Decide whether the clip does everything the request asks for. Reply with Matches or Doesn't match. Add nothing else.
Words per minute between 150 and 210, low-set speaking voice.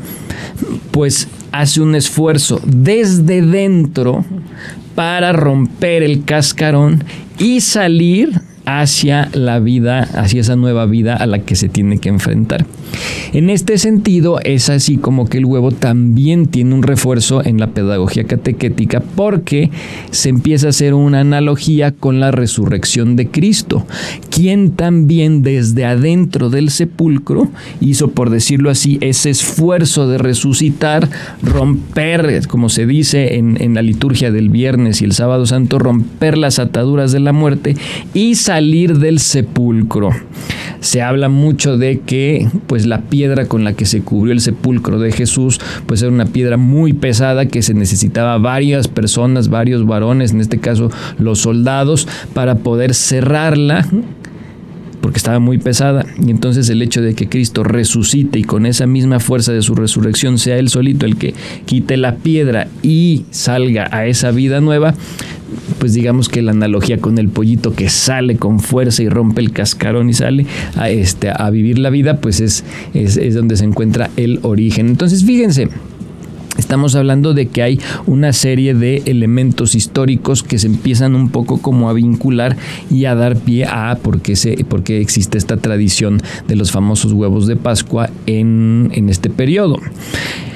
Matches